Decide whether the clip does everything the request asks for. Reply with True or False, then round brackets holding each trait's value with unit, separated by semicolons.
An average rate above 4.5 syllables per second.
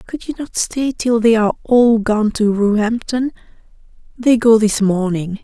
False (4.4 syllables/s)